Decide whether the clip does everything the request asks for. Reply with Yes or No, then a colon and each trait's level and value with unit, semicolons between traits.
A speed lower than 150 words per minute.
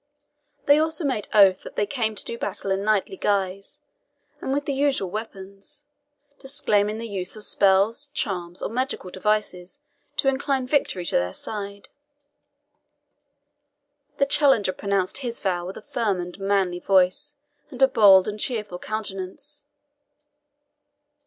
Yes: average, 140 wpm